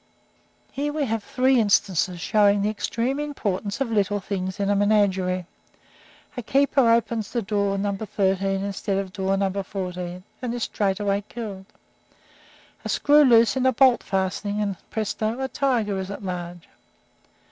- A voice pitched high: Yes, high, 205 Hz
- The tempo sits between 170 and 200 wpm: No, average, 155 wpm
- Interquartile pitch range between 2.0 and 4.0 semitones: Yes, average, 3.3 semitones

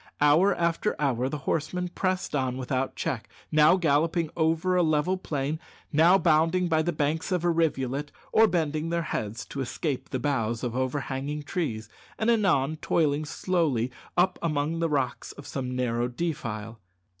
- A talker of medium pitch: Yes, medium, 150 Hz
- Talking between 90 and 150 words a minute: No, average, 160 wpm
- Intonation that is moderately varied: Yes, average, 4.1 semitones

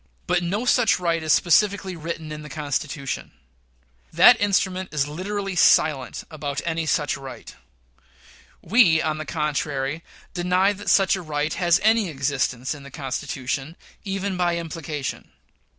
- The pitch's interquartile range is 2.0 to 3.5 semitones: No, average, 4.2 semitones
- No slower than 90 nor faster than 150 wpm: Yes, average, 140 wpm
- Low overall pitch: No, medium, 160 Hz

